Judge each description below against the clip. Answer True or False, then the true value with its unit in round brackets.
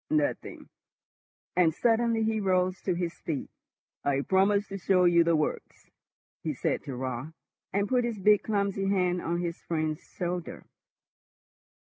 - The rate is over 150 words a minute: False (145 wpm)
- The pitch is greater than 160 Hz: True (185 Hz)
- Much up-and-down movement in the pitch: False (3.3 semitones)